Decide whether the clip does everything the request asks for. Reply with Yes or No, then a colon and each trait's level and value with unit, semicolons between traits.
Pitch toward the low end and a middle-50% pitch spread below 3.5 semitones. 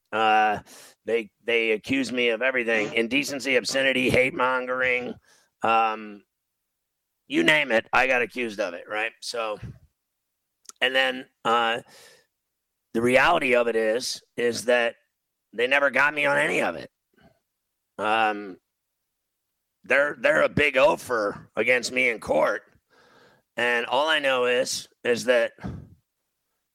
Yes: low, 120 Hz; average, 2.7 semitones